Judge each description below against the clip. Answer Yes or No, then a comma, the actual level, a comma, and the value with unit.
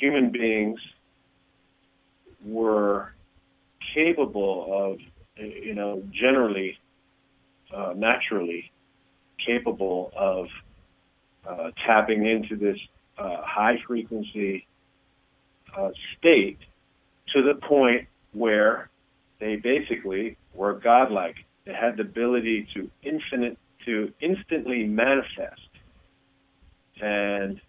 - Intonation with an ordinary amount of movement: Yes, average, 3.5 semitones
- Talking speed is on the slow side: Yes, slow, 80 wpm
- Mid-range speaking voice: No, low, 105 Hz